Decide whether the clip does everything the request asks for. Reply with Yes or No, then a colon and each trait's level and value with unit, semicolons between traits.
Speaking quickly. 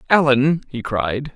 No: slow, 135 wpm